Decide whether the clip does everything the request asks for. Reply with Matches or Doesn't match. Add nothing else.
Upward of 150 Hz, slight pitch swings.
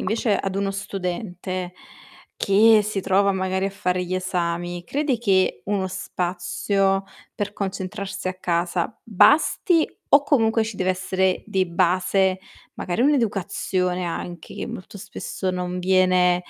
Matches